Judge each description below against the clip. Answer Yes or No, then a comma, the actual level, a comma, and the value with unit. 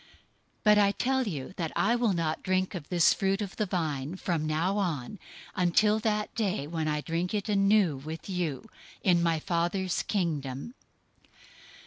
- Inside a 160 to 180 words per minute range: Yes, average, 165 wpm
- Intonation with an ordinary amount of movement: Yes, average, 4.3 semitones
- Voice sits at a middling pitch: Yes, medium, 180 Hz